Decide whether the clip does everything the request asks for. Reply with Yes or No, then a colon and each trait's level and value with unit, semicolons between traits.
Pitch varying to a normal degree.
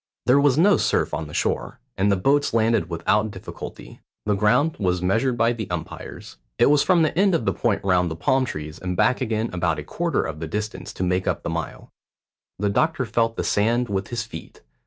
No: wide, 5.9 semitones